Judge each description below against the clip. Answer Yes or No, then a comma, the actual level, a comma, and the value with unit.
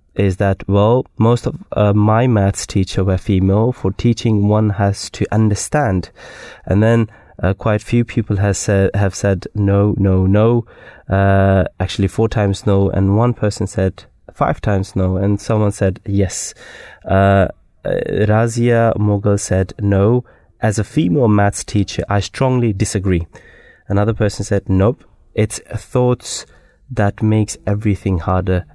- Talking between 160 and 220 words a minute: No, average, 150 wpm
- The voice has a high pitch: No, low, 100 Hz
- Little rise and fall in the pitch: Yes, narrow, 2.2 semitones